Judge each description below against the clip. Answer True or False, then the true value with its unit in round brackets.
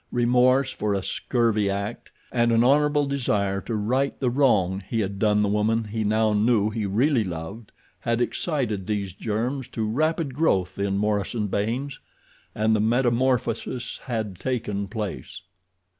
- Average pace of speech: True (145 wpm)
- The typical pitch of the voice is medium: False (110 Hz)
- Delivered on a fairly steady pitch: False (3.5 semitones)